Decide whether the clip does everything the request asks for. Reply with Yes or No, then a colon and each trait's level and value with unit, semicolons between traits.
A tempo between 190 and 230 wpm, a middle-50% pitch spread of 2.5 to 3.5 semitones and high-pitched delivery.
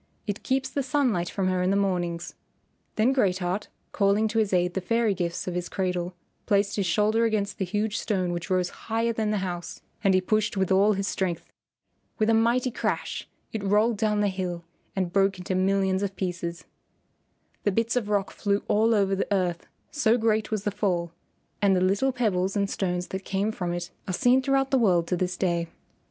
Yes: fast, 205 wpm; average, 3.0 semitones; high, 195 Hz